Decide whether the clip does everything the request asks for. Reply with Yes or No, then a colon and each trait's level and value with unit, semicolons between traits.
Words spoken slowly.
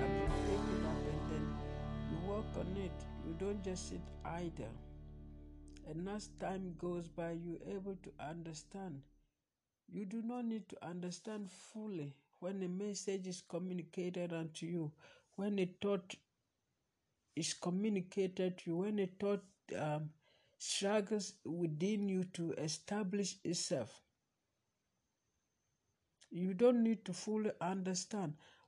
Yes: slow, 130 wpm